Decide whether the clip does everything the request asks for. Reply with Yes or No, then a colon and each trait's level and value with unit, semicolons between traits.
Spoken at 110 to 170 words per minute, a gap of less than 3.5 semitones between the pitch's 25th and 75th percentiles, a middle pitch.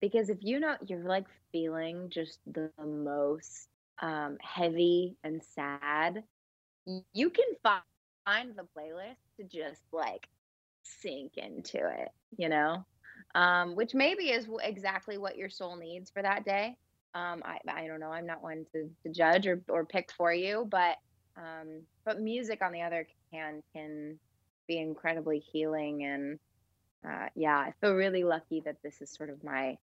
No: average, 160 wpm; average, 4.0 semitones; medium, 165 Hz